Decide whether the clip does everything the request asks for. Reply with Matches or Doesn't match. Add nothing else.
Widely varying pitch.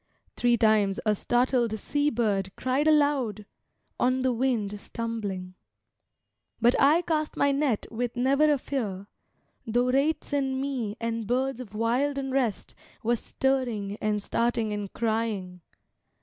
Doesn't match